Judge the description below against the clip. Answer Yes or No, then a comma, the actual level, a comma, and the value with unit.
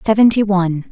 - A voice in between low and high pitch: No, high, 195 Hz